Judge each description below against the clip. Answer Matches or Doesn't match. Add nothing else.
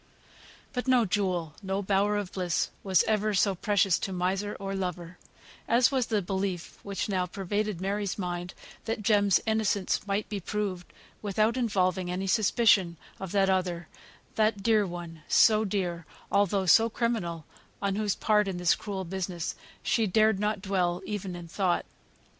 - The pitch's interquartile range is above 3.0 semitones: Doesn't match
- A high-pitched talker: Matches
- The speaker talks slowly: Doesn't match